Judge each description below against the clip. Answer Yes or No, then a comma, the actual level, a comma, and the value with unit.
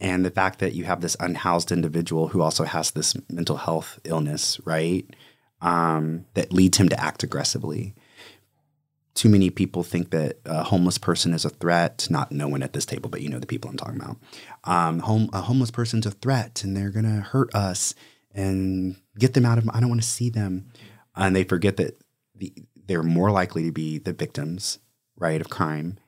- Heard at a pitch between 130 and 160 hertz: No, very low, 95 Hz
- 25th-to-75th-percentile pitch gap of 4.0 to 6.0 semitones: Yes, average, 4.3 semitones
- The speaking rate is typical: Yes, average, 195 wpm